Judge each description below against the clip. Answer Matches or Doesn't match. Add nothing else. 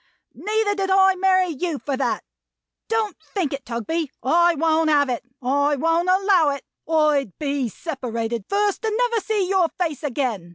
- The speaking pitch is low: Doesn't match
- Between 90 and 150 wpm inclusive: Doesn't match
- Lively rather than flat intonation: Matches